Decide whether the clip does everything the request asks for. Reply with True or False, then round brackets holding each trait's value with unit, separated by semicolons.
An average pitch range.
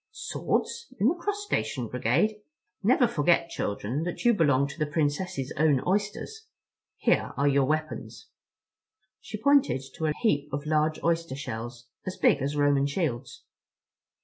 False (6.7 semitones)